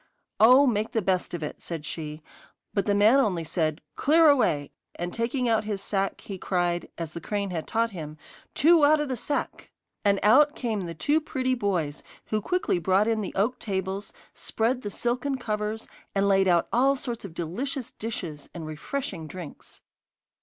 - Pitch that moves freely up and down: Yes, wide, 6.0 semitones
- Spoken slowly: No, average, 180 wpm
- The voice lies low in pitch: No, high, 205 Hz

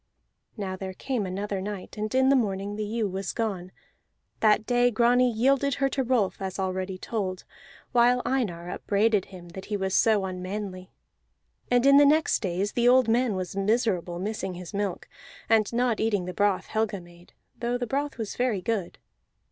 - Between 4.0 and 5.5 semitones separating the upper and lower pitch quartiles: Yes, average, 4.3 semitones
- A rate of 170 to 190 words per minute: Yes, average, 180 wpm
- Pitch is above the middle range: Yes, high, 210 Hz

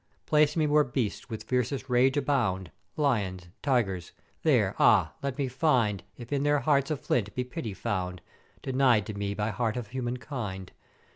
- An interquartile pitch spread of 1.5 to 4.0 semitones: No, average, 5.1 semitones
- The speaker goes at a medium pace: Yes, average, 170 wpm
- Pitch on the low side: Yes, low, 125 Hz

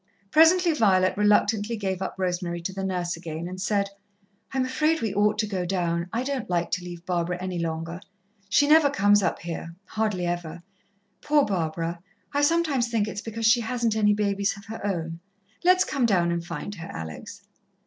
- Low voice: No, high, 200 Hz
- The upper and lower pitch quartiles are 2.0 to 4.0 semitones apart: No, average, 4.7 semitones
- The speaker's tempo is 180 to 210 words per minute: Yes, average, 185 wpm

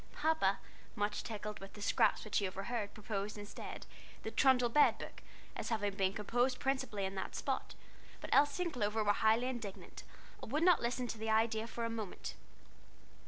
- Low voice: No, high, 220 Hz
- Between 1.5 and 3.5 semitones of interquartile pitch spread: Yes, average, 3.2 semitones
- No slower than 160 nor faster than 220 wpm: Yes, average, 180 wpm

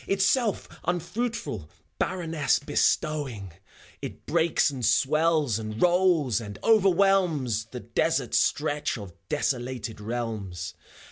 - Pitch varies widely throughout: Yes, wide, 7.7 semitones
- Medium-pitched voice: Yes, medium, 145 Hz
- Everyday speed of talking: No, slow, 95 wpm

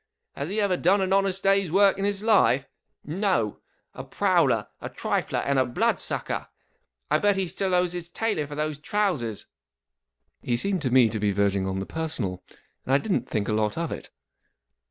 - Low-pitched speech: No, medium, 160 Hz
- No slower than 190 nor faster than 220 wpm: Yes, average, 200 wpm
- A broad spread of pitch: Yes, wide, 8.5 semitones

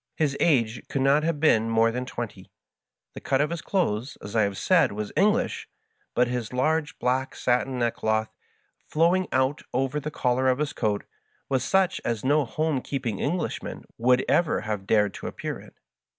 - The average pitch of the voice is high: No, low, 130 Hz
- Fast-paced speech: No, average, 180 wpm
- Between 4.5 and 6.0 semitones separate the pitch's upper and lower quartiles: Yes, average, 4.9 semitones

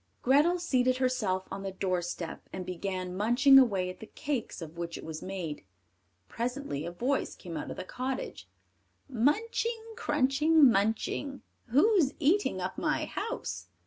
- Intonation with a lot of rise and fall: Yes, wide, 7.5 semitones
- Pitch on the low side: No, high, 245 Hz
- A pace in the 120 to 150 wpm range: Yes, average, 145 wpm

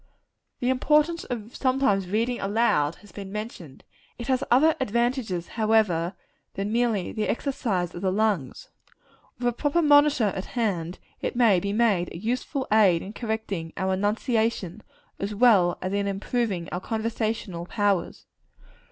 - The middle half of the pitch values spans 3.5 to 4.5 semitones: Yes, average, 4.1 semitones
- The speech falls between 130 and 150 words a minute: Yes, average, 145 wpm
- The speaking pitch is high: Yes, high, 215 Hz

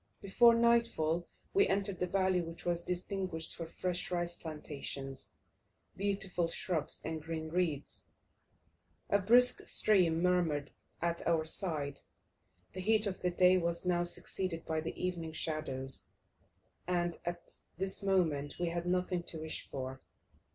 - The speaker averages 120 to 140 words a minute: Yes, slow, 135 wpm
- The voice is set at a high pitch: No, medium, 175 Hz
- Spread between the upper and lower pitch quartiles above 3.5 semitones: No, narrow, 2.6 semitones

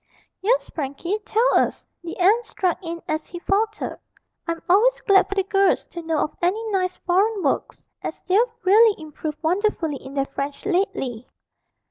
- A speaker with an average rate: Yes, average, 165 wpm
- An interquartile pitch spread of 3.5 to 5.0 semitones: Yes, average, 4.5 semitones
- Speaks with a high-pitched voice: Yes, very high, 365 Hz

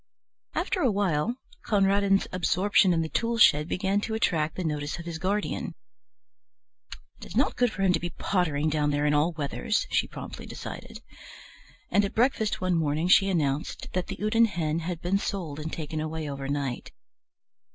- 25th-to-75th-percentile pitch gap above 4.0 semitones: Yes, average, 4.7 semitones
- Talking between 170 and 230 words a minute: Yes, average, 175 wpm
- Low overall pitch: No, medium, 175 Hz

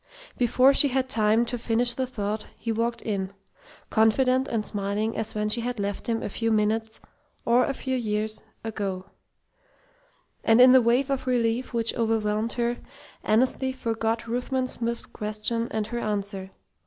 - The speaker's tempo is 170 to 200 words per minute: No, average, 160 wpm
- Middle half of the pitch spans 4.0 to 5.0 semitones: No, narrow, 2.5 semitones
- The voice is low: No, high, 230 Hz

